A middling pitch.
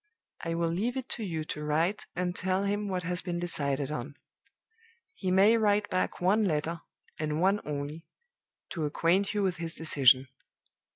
Yes: medium, 175 Hz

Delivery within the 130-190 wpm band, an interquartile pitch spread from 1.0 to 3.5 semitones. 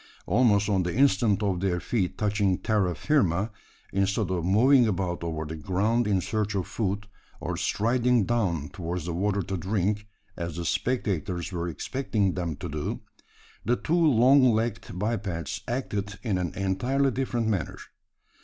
No: average, 155 wpm; average, 4.3 semitones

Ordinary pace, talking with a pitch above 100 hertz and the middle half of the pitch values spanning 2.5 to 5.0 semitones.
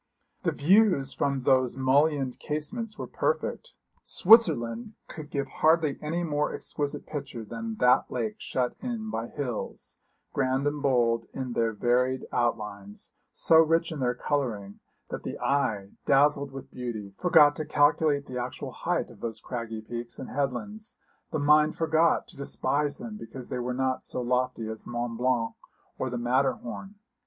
Yes: average, 155 wpm; low, 135 Hz; average, 3.9 semitones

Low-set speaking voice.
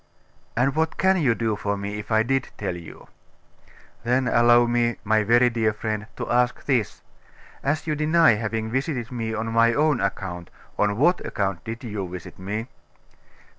Yes: low, 115 Hz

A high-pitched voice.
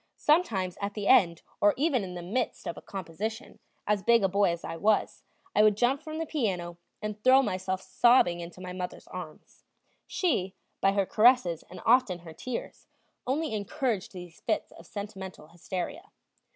Yes: high, 200 Hz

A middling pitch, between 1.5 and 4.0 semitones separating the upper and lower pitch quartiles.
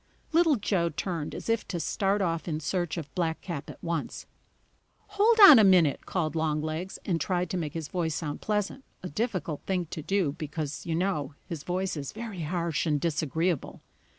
Yes: medium, 170 Hz; average, 3.6 semitones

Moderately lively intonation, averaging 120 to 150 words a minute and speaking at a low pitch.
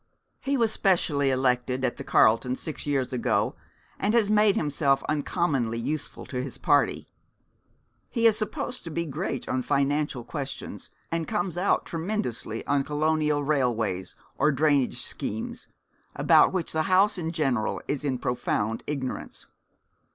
No: average, 4.7 semitones; average, 145 wpm; medium, 145 Hz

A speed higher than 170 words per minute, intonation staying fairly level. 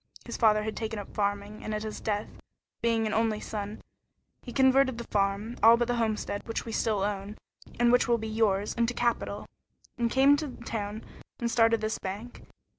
Yes: average, 190 wpm; narrow, 2.0 semitones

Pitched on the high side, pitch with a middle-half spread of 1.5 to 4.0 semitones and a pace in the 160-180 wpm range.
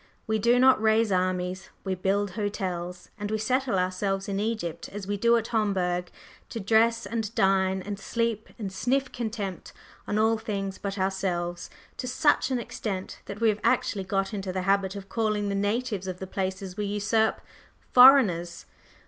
Yes: high, 200 Hz; average, 2.8 semitones; average, 175 wpm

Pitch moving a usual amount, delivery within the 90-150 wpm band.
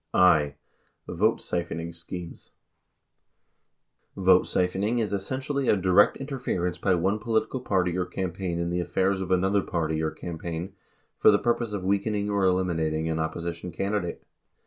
Yes: average, 3.1 semitones; average, 145 wpm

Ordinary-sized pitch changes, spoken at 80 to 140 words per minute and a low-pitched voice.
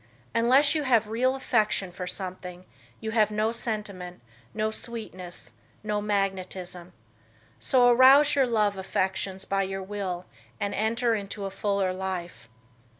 No: average, 3.6 semitones; slow, 135 wpm; high, 205 Hz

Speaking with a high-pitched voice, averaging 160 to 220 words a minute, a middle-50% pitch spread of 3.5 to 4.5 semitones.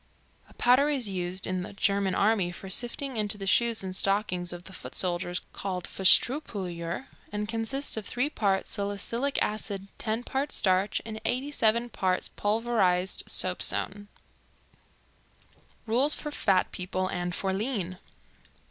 No: high, 200 Hz; average, 140 wpm; average, 4.0 semitones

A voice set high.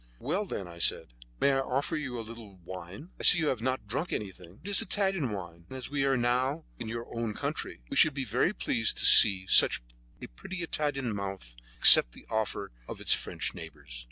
No: low, 120 Hz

